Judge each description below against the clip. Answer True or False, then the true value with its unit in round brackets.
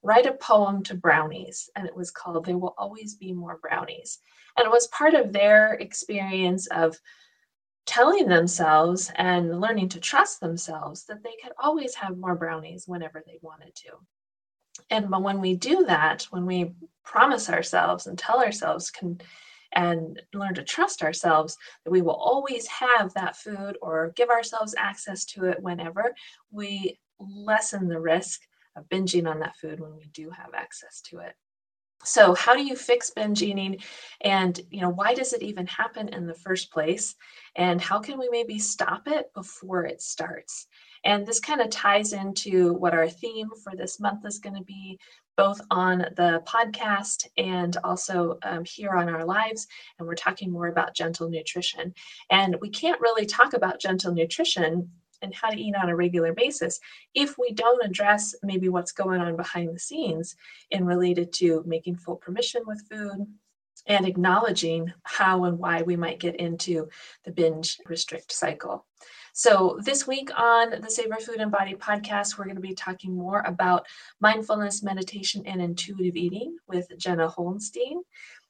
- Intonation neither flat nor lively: True (3.8 semitones)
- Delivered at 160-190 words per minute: True (170 wpm)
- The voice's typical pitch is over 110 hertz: True (185 Hz)